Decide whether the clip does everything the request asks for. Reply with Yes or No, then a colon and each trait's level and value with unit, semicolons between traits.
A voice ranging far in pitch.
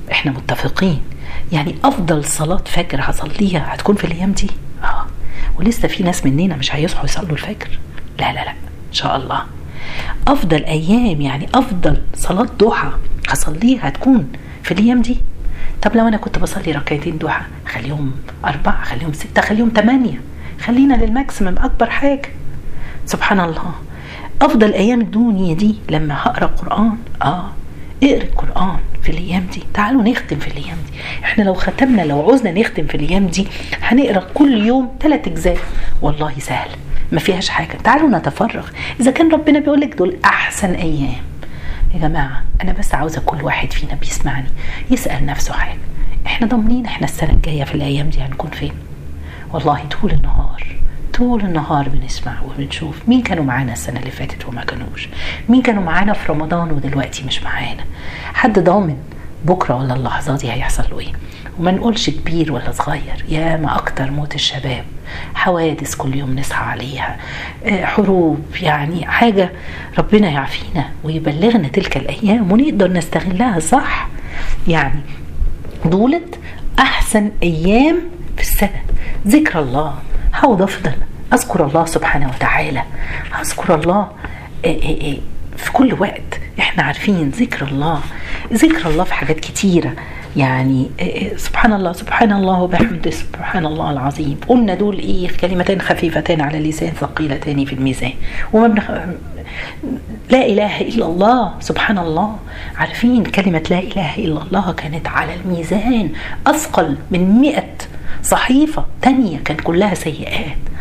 Yes: wide, 7.5 semitones